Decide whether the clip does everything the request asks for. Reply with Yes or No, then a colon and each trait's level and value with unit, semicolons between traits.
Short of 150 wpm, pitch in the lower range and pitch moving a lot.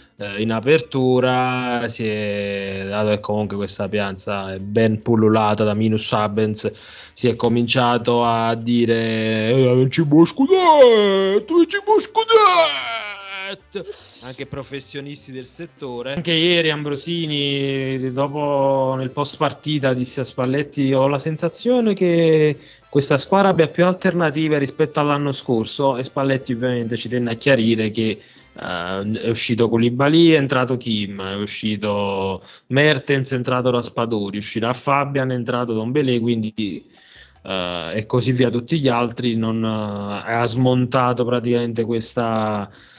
No: average, 130 wpm; low, 125 Hz; average, 4.6 semitones